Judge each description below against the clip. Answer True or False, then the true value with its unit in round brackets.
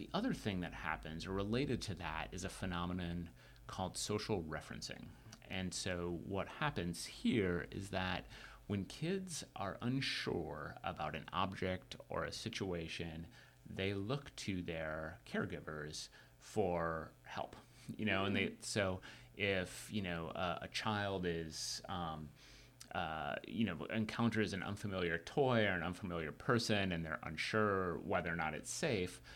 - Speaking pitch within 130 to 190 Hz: False (95 Hz)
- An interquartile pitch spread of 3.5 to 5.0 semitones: True (4.1 semitones)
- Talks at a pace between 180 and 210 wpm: False (145 wpm)